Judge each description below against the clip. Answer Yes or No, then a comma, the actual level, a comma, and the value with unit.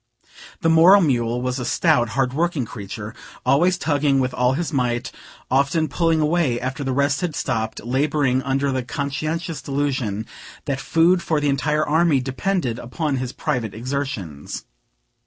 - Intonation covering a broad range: No, average, 3.8 semitones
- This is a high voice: No, low, 135 Hz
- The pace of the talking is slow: No, average, 155 wpm